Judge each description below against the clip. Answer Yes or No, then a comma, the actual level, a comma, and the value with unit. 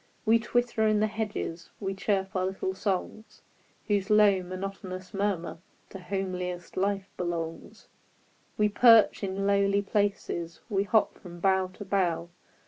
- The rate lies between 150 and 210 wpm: No, slow, 135 wpm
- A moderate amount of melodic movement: No, narrow, 2.0 semitones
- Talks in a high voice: Yes, high, 195 Hz